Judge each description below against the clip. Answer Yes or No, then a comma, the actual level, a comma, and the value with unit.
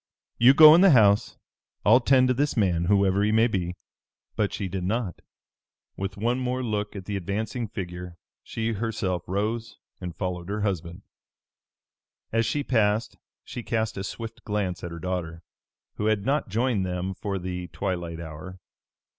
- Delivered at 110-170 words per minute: Yes, average, 165 wpm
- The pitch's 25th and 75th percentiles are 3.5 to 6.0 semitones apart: Yes, average, 3.8 semitones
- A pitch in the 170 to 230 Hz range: No, low, 100 Hz